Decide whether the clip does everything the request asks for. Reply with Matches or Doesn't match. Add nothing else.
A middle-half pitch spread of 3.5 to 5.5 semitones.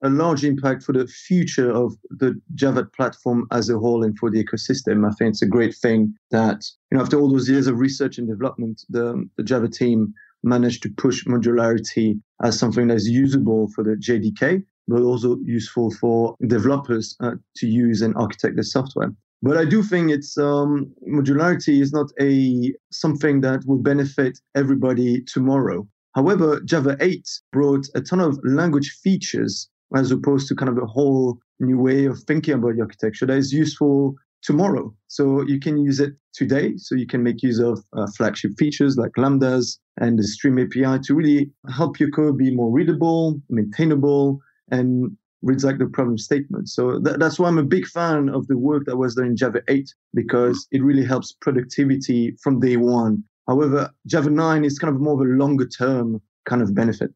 Doesn't match